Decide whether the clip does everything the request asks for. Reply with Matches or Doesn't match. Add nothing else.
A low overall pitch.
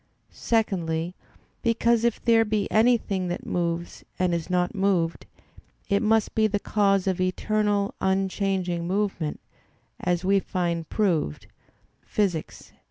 Doesn't match